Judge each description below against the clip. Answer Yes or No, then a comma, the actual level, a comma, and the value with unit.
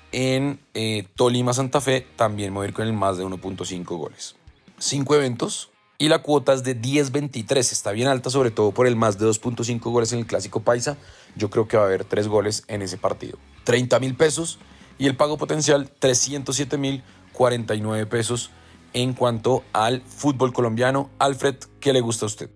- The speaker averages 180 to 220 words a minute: Yes, average, 185 wpm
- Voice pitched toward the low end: Yes, low, 125 Hz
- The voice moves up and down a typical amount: Yes, average, 4.3 semitones